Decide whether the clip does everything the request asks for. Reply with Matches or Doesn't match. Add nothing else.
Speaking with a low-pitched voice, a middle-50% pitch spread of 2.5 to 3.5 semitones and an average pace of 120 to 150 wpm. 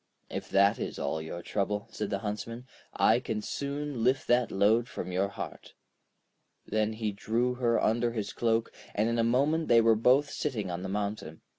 Doesn't match